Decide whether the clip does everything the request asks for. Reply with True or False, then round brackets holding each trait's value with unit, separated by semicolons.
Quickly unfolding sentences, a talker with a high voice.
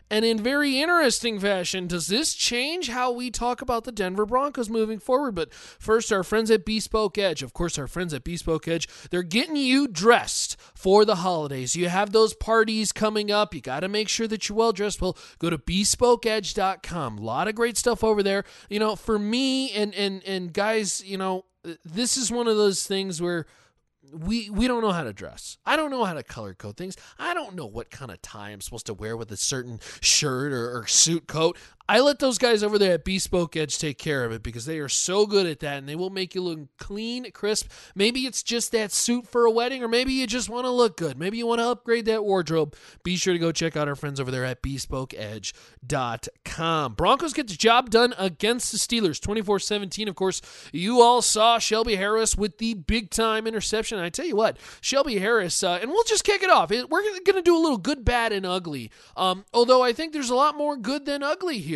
True (225 wpm; 210 Hz)